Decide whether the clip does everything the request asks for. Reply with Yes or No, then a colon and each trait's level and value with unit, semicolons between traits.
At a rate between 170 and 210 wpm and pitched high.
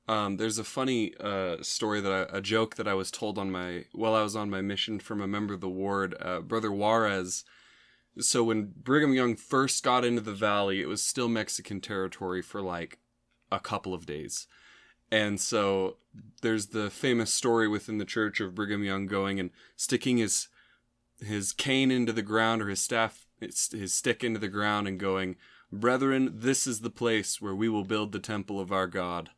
No: average, 195 wpm; low, 105 Hz